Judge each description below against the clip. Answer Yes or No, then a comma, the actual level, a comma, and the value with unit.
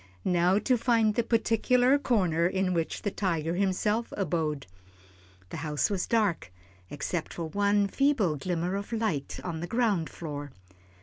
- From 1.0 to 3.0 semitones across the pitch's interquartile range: No, average, 5.2 semitones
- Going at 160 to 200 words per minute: No, average, 145 wpm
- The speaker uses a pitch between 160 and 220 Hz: Yes, high, 190 Hz